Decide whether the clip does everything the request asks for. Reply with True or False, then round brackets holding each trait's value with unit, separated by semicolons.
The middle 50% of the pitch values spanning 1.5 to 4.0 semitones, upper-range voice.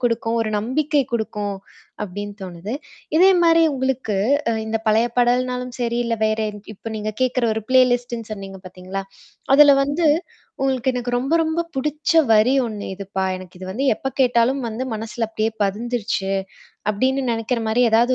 True (3.4 semitones; 235 Hz)